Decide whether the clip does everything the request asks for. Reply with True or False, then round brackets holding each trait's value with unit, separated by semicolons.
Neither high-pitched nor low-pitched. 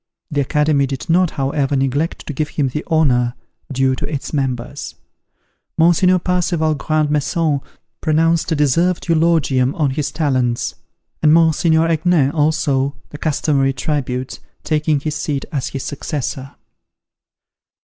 True (150 Hz)